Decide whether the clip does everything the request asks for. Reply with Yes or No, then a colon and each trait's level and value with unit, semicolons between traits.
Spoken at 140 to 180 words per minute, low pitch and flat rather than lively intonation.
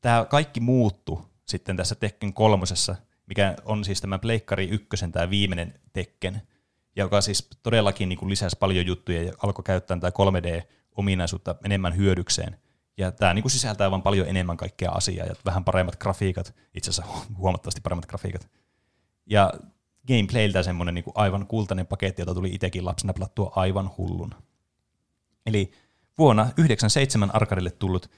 Yes: average, 150 wpm; very low, 95 Hz; narrow, 2.3 semitones